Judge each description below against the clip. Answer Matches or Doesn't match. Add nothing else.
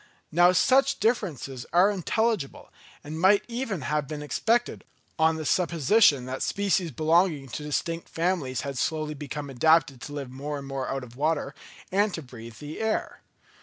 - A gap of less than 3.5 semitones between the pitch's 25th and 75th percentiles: Doesn't match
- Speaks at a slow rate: Doesn't match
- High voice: Doesn't match